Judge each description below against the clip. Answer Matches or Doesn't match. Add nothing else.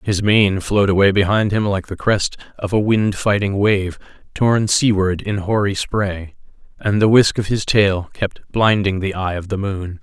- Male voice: Matches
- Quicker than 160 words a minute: Matches